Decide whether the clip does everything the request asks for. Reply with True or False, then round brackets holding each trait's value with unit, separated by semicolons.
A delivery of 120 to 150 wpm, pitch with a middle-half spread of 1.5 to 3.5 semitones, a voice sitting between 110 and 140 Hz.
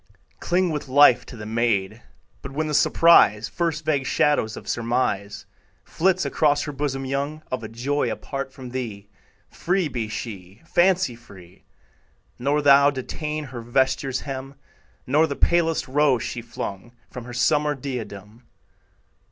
False (145 wpm; 4.1 semitones; 135 Hz)